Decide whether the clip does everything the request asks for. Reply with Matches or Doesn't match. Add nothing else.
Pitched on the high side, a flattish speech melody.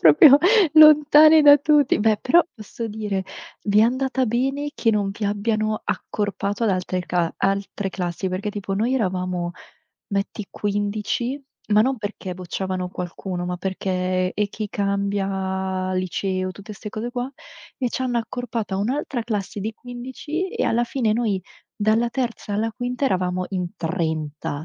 Doesn't match